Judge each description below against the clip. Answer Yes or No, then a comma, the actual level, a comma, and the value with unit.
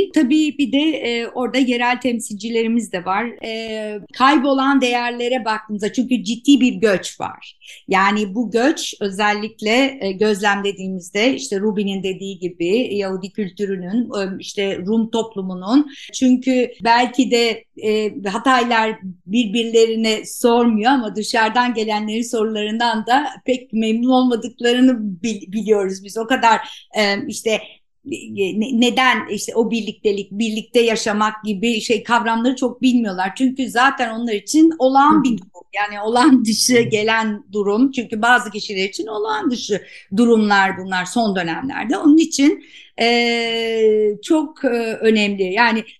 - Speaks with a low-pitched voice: No, high, 225 Hz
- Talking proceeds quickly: No, average, 125 wpm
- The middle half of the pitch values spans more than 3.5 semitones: No, average, 3.0 semitones